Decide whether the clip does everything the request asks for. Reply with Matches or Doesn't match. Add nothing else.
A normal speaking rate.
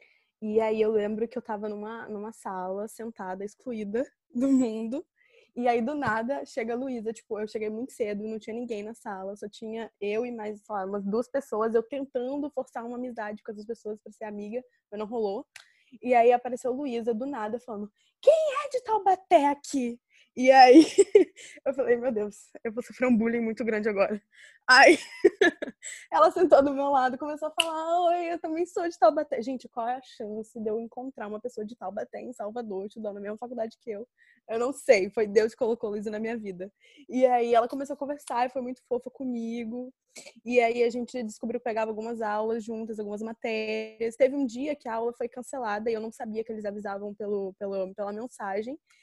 Doesn't match